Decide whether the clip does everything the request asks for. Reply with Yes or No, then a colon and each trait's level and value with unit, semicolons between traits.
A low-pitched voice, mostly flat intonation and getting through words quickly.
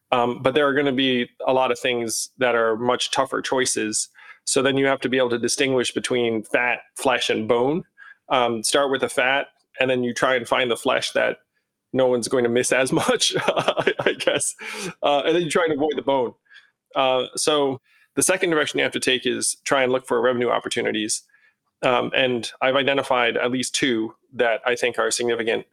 Yes: low, 125 Hz; narrow, 2.1 semitones; fast, 210 wpm